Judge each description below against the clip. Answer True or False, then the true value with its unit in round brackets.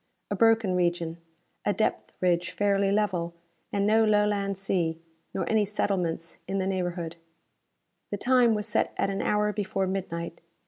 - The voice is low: False (195 Hz)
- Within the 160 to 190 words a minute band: False (150 wpm)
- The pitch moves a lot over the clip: False (3.0 semitones)